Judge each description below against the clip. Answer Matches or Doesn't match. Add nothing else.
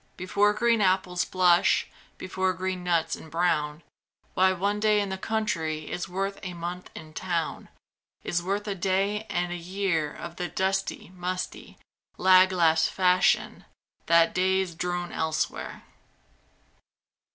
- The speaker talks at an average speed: Doesn't match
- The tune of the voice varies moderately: Doesn't match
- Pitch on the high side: Doesn't match